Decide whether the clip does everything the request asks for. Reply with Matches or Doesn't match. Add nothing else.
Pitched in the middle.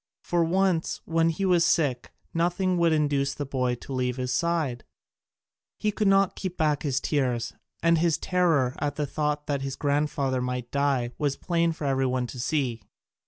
Matches